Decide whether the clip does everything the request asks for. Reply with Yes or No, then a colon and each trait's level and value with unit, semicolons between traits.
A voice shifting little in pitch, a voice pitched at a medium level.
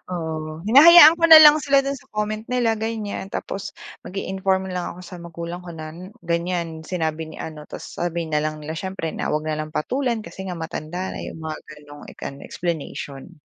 No: average, 4.8 semitones; medium, 175 Hz